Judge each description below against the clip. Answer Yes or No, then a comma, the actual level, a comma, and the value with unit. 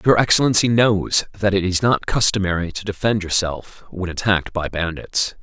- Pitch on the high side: No, low, 100 Hz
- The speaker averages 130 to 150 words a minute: No, average, 165 wpm